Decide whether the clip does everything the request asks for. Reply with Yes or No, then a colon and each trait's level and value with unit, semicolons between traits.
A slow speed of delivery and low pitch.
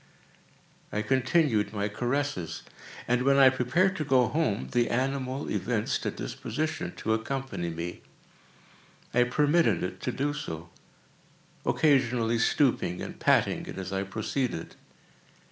Yes: slow, 130 wpm; low, 125 Hz